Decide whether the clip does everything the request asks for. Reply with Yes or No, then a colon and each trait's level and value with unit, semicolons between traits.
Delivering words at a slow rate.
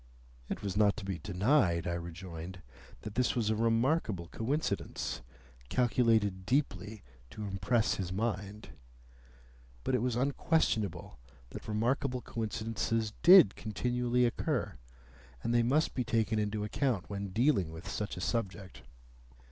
Yes: slow, 130 wpm